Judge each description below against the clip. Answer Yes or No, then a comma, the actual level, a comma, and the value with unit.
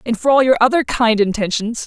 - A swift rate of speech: Yes, fast, 225 wpm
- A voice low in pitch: No, high, 235 Hz